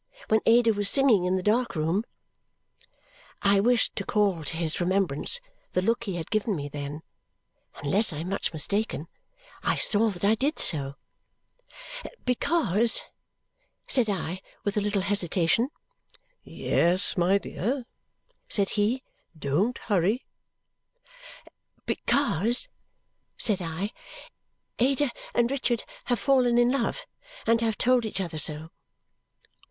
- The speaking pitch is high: Yes, high, 205 Hz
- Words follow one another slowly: Yes, slow, 130 wpm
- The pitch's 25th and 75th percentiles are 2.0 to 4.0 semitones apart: No, average, 5.2 semitones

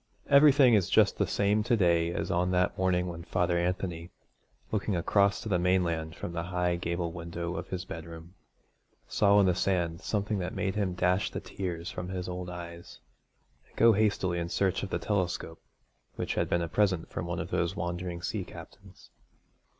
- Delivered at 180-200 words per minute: Yes, average, 190 wpm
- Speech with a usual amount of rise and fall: No, narrow, 2.3 semitones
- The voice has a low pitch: Yes, very low, 90 Hz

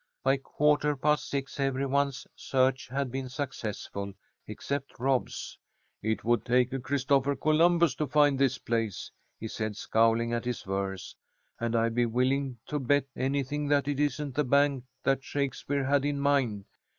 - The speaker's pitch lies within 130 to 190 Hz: Yes, low, 135 Hz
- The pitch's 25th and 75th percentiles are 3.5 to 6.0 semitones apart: No, average, 3.0 semitones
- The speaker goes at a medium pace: Yes, average, 160 wpm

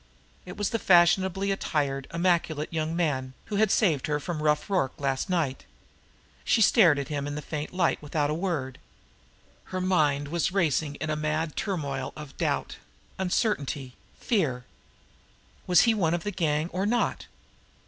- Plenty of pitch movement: No, average, 4.2 semitones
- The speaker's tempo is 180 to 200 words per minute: No, average, 160 wpm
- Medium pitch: Yes, medium, 160 Hz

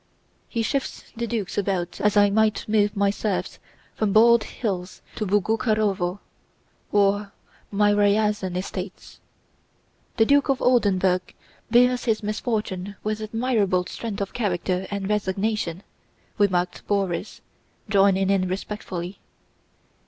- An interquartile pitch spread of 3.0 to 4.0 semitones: No, narrow, 2.4 semitones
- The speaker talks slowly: Yes, slow, 115 wpm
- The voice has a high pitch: Yes, high, 205 Hz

